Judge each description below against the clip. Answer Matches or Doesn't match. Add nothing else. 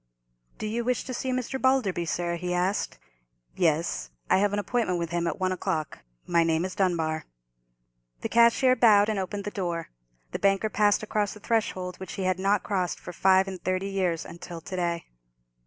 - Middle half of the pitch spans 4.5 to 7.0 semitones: Doesn't match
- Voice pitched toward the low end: Doesn't match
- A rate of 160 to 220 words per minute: Matches